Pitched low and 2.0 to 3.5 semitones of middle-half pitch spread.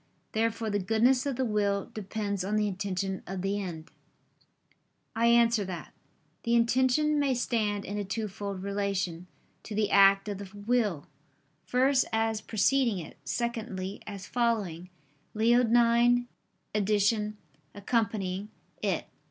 No: high, 210 Hz; average, 3.0 semitones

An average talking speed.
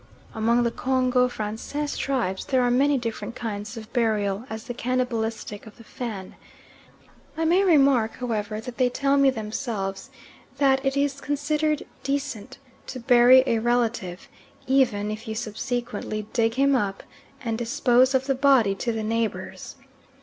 Yes: average, 150 wpm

